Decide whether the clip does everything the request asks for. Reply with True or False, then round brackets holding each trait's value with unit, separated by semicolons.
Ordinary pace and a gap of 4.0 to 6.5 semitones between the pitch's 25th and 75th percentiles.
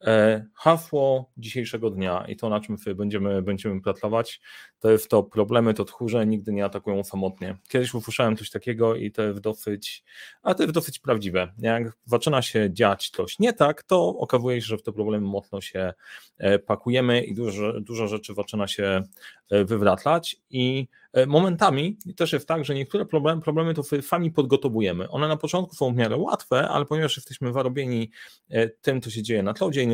False (175 wpm; 5.1 semitones)